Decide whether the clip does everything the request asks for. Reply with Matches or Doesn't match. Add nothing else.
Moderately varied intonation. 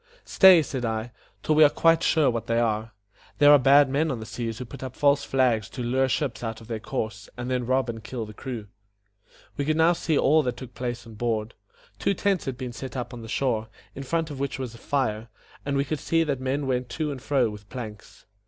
Matches